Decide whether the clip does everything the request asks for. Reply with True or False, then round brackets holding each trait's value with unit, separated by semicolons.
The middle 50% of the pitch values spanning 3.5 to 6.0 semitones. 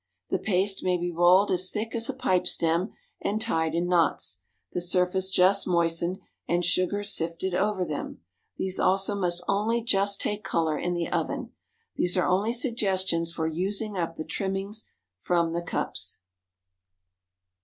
False (2.7 semitones)